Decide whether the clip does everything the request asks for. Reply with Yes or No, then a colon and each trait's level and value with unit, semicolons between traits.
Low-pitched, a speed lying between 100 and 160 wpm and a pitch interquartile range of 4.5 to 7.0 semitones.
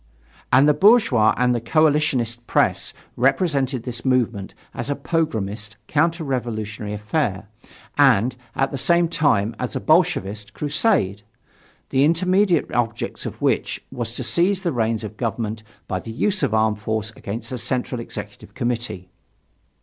Yes: low, 120 Hz; average, 145 wpm; wide, 5.5 semitones